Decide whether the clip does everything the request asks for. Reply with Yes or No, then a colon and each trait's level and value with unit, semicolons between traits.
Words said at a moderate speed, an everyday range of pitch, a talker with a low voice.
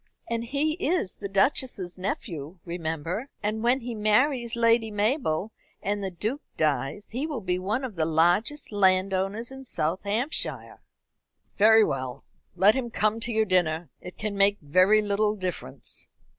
No: average, 155 wpm; average, 4.2 semitones; high, 205 Hz